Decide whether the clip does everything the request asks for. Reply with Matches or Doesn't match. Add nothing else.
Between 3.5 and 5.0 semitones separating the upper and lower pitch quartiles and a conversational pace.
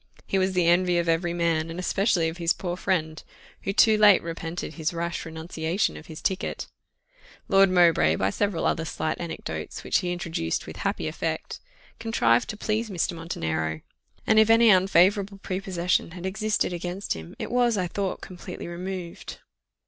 Doesn't match